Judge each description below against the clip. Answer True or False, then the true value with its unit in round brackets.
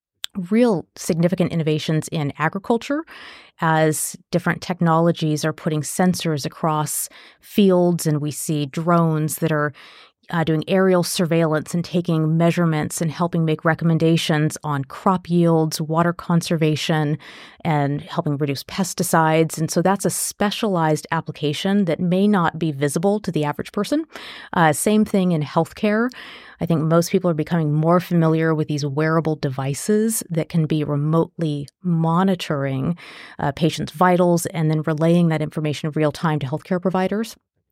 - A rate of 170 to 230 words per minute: False (145 wpm)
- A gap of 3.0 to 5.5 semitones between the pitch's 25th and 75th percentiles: False (2.6 semitones)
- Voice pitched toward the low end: False (165 Hz)